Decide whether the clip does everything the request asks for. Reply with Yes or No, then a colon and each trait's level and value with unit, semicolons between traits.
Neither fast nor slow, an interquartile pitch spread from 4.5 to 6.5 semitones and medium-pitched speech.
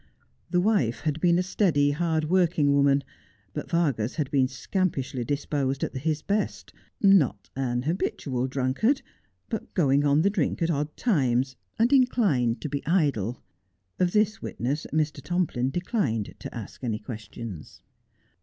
Yes: average, 145 wpm; wide, 5.4 semitones; medium, 145 Hz